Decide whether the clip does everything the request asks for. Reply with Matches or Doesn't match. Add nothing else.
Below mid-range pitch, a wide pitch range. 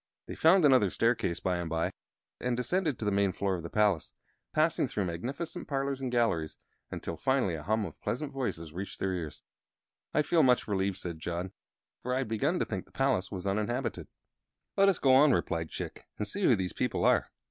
Matches